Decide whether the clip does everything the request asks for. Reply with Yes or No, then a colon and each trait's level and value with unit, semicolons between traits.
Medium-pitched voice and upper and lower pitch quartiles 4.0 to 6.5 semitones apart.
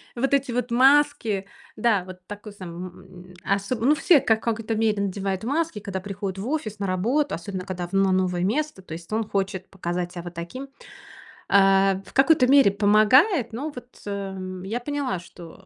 No: high, 205 Hz; average, 4.8 semitones